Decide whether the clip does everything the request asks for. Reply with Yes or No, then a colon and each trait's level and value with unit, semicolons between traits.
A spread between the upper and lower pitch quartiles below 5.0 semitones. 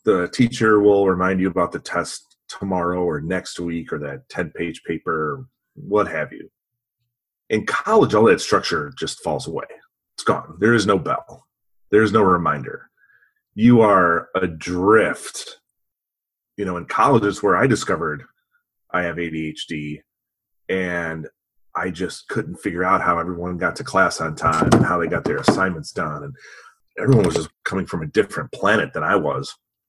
No: wide, 5.4 semitones